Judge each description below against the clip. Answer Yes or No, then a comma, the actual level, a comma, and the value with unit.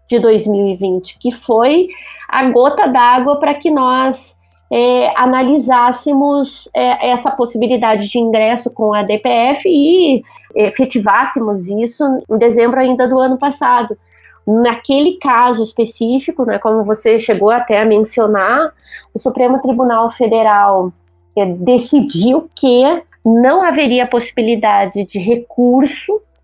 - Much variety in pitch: No, average, 3.3 semitones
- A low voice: No, high, 245 Hz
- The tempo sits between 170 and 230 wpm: No, slow, 120 wpm